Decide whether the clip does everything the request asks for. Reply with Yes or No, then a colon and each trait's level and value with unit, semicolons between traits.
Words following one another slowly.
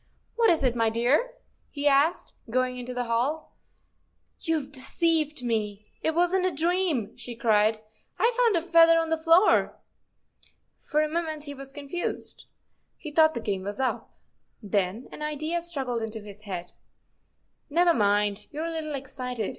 No: average, 175 wpm